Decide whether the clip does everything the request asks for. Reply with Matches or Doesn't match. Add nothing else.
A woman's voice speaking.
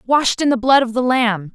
Matches